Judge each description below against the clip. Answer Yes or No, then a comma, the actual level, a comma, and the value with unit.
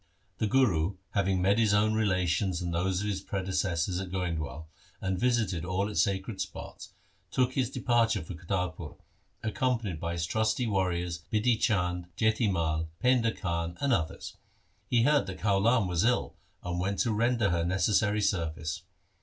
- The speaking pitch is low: Yes, very low, 95 Hz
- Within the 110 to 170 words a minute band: Yes, average, 160 wpm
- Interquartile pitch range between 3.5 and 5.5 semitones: Yes, average, 4.1 semitones